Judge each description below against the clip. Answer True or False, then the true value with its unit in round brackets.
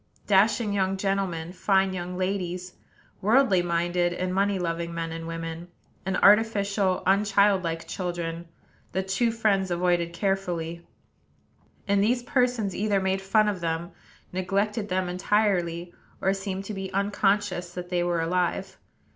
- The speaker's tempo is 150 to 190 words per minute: False (135 wpm)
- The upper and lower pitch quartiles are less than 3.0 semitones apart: True (2.4 semitones)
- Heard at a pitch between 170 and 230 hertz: True (190 Hz)